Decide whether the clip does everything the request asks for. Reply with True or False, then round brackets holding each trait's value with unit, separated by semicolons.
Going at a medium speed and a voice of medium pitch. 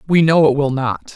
False (260 wpm; 145 Hz)